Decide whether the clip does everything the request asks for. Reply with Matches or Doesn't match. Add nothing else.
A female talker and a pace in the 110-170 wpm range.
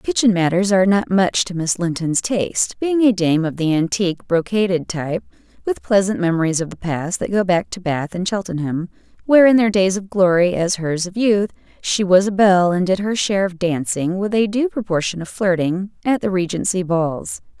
Doesn't match